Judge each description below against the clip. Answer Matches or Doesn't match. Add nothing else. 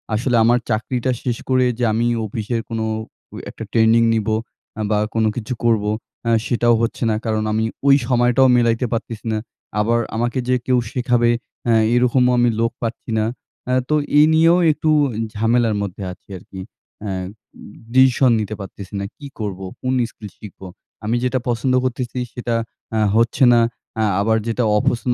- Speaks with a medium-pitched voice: Doesn't match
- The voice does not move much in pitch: Matches